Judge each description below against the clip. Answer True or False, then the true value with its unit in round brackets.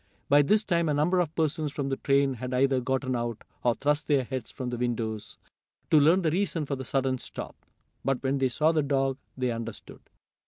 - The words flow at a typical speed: False (210 wpm)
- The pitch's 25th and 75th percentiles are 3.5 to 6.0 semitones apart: False (3.0 semitones)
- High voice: False (135 Hz)